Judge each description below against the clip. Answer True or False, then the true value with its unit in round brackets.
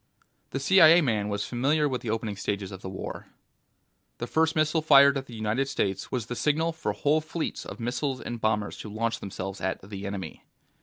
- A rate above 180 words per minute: True (200 wpm)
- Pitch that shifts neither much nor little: False (6.3 semitones)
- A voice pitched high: False (120 Hz)